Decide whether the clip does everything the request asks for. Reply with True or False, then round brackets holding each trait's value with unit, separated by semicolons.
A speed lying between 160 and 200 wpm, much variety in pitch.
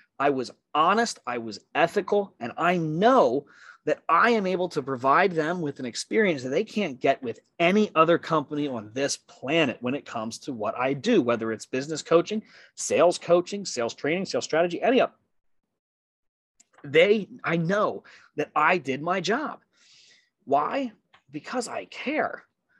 True (165 wpm; 6.6 semitones)